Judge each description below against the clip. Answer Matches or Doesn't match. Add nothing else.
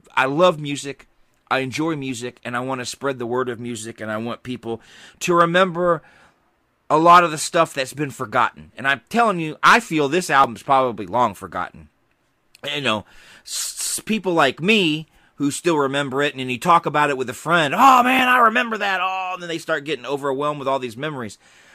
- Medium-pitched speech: Matches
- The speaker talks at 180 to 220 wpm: Matches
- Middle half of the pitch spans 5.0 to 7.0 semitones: Matches